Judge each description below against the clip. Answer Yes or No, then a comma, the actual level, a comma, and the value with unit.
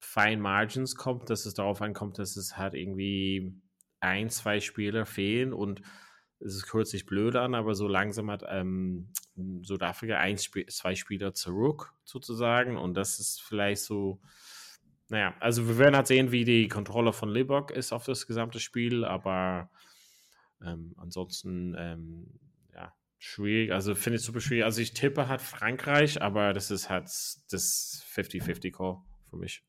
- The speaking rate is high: No, average, 155 wpm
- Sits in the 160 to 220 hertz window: No, low, 105 Hz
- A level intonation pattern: No, average, 3.5 semitones